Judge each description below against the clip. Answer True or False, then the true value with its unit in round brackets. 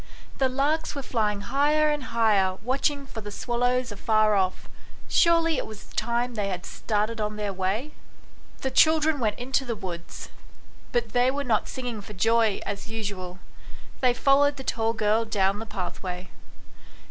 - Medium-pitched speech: False (225 Hz)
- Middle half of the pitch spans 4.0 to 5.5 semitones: True (4.3 semitones)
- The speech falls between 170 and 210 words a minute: False (160 wpm)